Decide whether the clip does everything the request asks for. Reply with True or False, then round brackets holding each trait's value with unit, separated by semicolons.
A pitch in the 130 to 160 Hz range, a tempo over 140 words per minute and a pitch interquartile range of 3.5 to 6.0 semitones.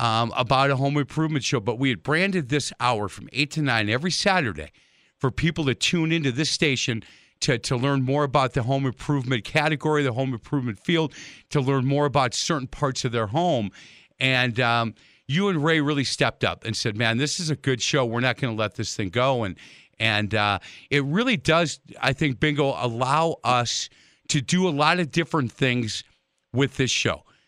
True (135 Hz; 200 wpm; 3.9 semitones)